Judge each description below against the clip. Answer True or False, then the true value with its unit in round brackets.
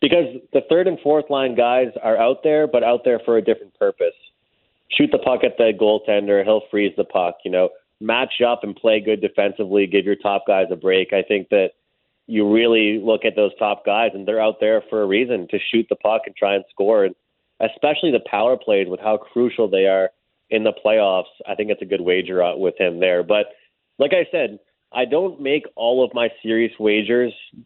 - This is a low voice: True (110 Hz)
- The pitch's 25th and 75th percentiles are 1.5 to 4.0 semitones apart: False (5.1 semitones)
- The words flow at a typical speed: False (220 wpm)